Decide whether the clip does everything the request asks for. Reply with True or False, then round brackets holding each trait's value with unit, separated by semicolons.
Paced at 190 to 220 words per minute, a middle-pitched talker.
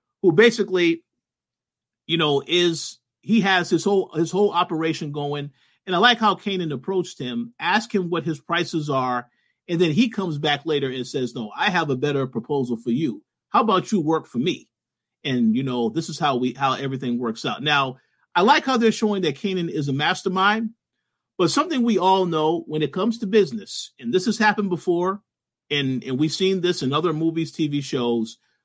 True (200 wpm; 165 Hz)